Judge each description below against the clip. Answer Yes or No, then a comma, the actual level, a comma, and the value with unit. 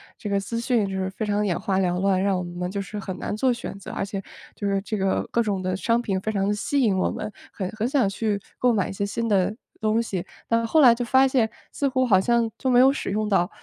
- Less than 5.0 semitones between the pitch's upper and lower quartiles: Yes, average, 3.2 semitones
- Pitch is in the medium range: No, high, 205 Hz